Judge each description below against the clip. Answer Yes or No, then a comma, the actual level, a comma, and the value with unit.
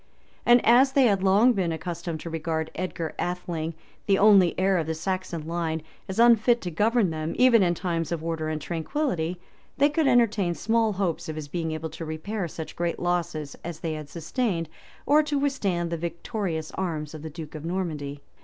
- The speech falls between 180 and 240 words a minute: Yes, average, 190 wpm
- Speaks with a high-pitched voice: No, medium, 175 Hz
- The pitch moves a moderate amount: Yes, average, 4.4 semitones